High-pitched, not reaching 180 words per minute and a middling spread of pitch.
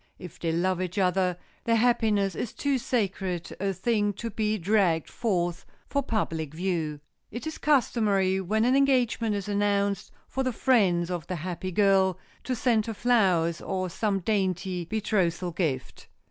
Yes: high, 195 Hz; average, 160 wpm; average, 3.7 semitones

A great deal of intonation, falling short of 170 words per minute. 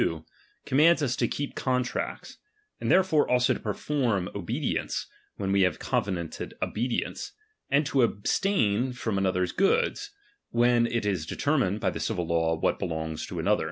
Yes: wide, 6.3 semitones; average, 155 wpm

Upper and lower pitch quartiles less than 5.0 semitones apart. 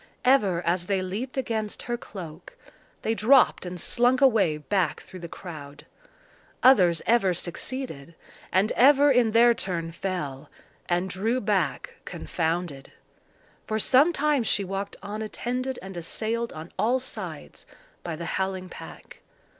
No: wide, 5.6 semitones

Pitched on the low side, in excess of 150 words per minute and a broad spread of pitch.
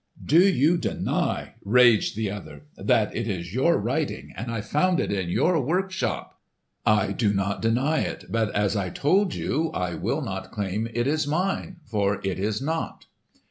Yes: low, 115 Hz; average, 175 wpm; wide, 7.5 semitones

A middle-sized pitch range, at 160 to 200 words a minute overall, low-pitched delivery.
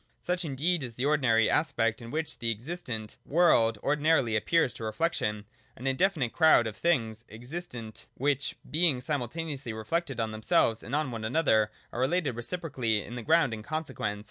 No: wide, 5.9 semitones; average, 165 wpm; low, 130 Hz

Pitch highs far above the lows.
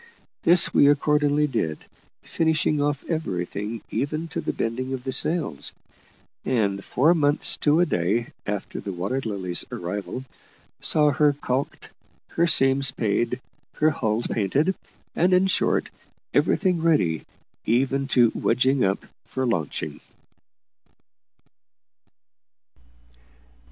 Yes: wide, 5.8 semitones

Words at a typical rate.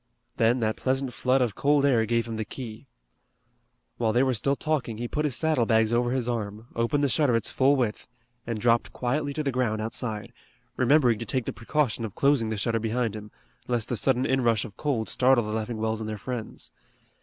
No: fast, 210 wpm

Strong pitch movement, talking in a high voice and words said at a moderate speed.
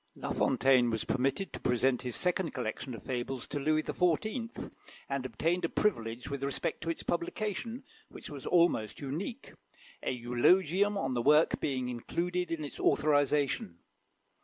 No: wide, 5.9 semitones; medium, 145 Hz; average, 155 wpm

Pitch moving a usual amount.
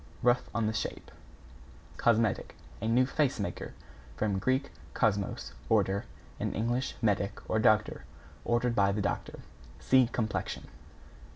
Yes: average, 3.0 semitones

